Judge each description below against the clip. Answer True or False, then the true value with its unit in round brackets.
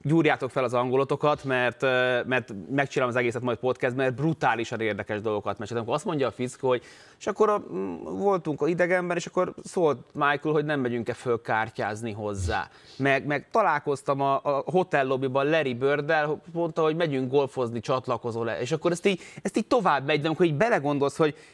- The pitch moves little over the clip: False (4.0 semitones)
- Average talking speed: False (180 wpm)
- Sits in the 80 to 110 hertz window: False (135 Hz)